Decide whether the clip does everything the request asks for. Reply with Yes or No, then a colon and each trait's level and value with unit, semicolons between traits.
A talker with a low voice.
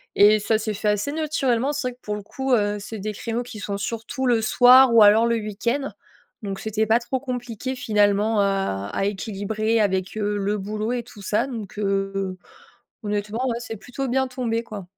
No: high, 220 Hz